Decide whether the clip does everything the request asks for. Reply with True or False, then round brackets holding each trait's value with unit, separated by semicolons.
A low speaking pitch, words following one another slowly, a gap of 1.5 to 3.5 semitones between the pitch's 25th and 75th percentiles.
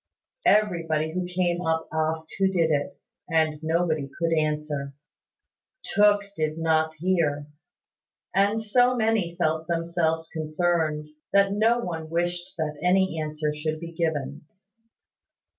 False (165 Hz; 125 wpm; 2.5 semitones)